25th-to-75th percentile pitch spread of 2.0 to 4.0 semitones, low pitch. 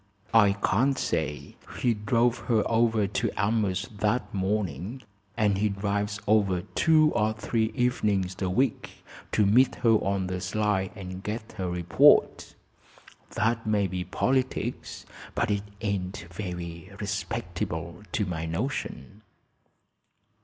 Yes: average, 3.2 semitones; low, 105 Hz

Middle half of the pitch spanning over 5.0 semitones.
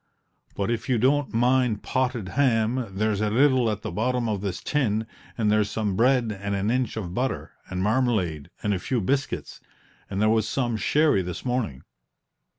No: average, 3.8 semitones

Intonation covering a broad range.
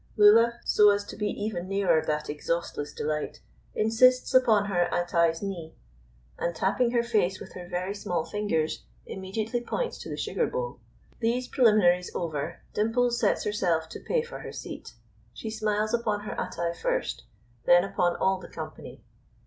No: average, 4.5 semitones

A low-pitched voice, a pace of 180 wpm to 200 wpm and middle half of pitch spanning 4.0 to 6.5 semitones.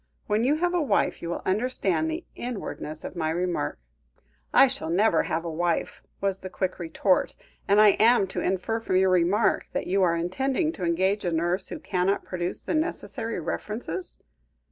No: high, 190 Hz; average, 185 wpm; average, 4.6 semitones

